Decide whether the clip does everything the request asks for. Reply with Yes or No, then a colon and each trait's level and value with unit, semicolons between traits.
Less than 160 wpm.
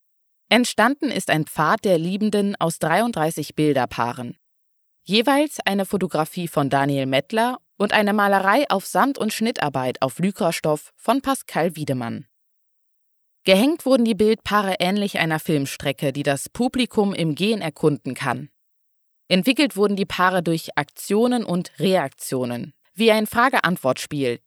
Yes: average, 130 wpm